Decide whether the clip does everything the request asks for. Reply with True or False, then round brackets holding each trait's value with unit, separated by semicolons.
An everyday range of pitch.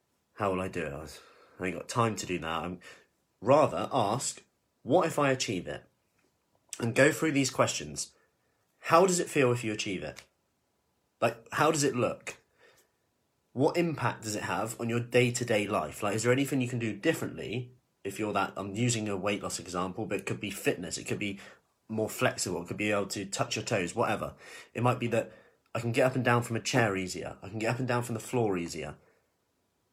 True (3.9 semitones)